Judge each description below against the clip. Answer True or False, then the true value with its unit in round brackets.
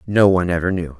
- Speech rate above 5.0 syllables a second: True (7.1 syllables/s)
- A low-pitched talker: True (90 Hz)